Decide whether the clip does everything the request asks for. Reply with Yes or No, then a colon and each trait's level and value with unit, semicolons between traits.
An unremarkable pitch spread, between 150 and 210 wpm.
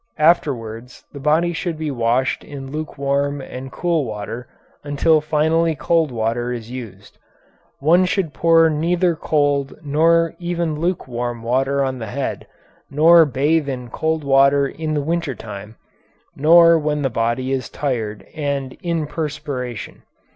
No: average, 4.0 semitones; average, 140 wpm